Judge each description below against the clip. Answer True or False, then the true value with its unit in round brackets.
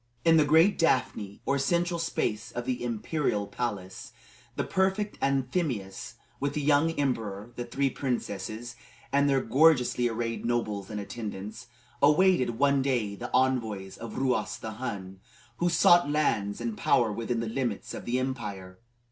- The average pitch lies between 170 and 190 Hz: False (125 Hz)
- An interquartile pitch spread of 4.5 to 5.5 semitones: True (4.8 semitones)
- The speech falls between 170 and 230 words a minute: False (150 wpm)